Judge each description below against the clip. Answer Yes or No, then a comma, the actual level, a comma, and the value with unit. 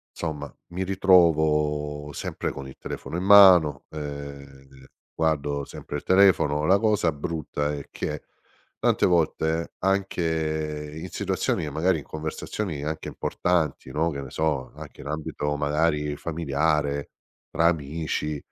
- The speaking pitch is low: Yes, very low, 75 Hz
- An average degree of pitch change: No, narrow, 2.3 semitones